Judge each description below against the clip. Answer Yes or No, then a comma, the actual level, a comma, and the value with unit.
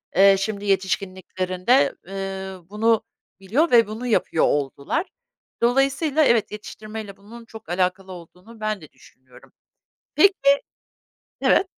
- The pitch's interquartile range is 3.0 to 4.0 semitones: Yes, average, 3.7 semitones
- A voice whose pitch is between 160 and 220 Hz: Yes, high, 200 Hz